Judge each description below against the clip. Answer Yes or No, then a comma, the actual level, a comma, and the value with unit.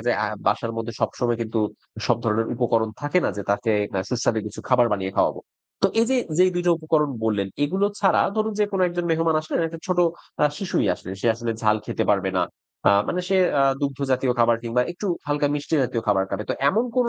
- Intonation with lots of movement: Yes, wide, 7.4 semitones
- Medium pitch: No, low, 130 Hz